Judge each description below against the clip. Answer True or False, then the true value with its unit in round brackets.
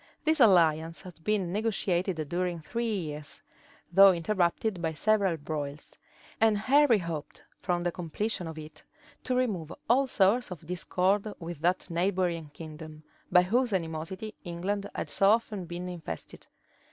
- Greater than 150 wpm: False (140 wpm)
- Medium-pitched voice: True (180 Hz)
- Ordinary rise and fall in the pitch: True (4.2 semitones)